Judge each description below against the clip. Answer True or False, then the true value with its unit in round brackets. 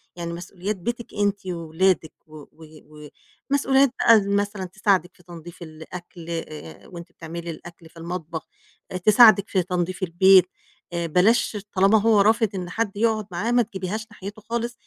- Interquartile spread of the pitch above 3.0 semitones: True (3.7 semitones)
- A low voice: False (185 Hz)